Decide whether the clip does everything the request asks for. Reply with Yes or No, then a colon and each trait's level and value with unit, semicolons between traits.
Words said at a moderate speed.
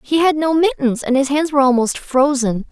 No: fast, 220 wpm